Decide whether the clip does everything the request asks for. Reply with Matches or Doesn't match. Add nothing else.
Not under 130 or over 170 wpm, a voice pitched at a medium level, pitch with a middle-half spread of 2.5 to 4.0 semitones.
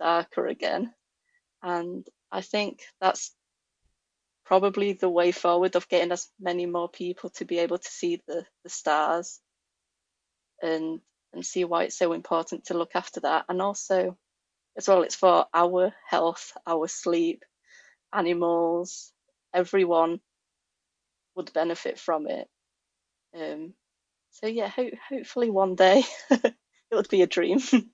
Matches